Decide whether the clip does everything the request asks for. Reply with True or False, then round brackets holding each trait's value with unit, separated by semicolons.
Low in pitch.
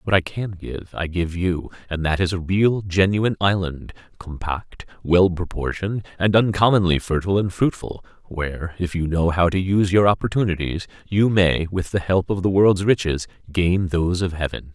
True (90 Hz)